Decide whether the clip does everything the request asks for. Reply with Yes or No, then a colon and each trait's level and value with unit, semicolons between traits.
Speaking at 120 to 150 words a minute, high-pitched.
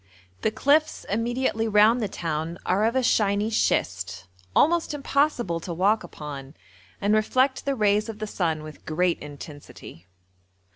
Yes: average, 145 wpm; high, 210 Hz